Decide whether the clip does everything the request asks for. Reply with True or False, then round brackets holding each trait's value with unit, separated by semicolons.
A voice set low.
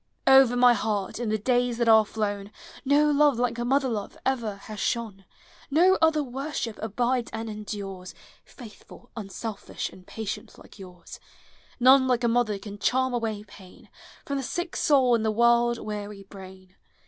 False (230 Hz)